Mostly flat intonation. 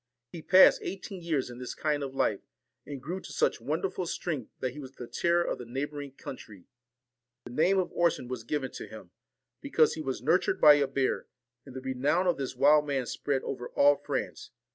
No: average, 3.9 semitones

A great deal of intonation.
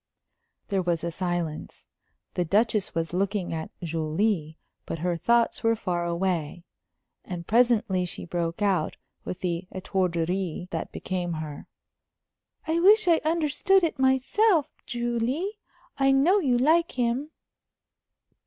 Yes: wide, 7.4 semitones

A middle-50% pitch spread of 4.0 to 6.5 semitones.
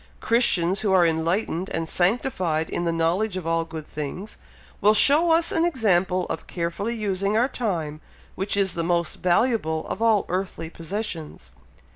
Yes: average, 4.6 semitones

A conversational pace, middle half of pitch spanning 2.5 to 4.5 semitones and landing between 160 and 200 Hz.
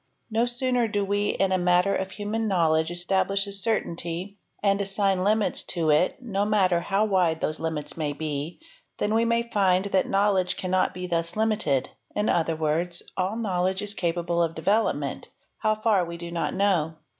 Yes: average, 170 wpm; average, 3.4 semitones; high, 190 Hz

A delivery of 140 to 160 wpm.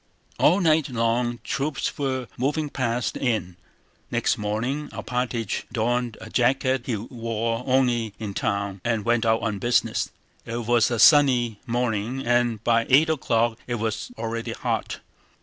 Yes: average, 150 wpm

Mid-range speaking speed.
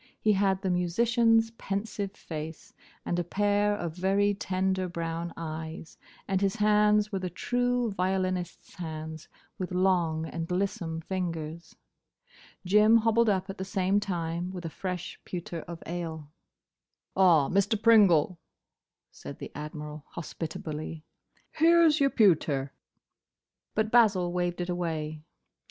No: slow, 130 wpm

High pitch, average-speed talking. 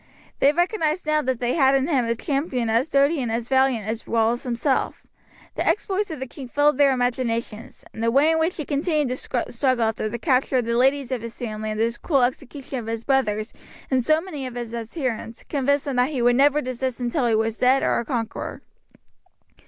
No: very high, 255 Hz; fast, 215 wpm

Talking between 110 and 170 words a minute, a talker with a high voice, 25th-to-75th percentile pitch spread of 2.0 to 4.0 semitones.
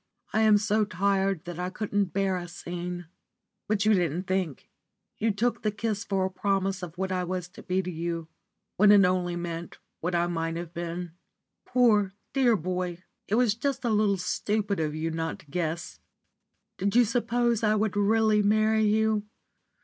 No: average, 180 wpm; high, 195 Hz; average, 3.4 semitones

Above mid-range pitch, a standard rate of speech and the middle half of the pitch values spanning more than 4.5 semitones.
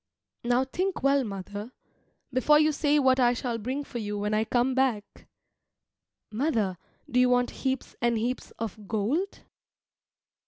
No: high, 245 Hz; average, 150 wpm; average, 3.6 semitones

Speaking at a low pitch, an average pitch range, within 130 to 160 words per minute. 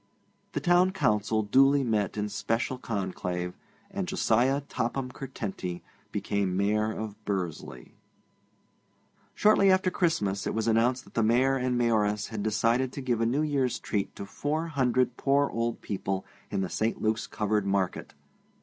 Yes: low, 115 Hz; average, 4.6 semitones; average, 150 wpm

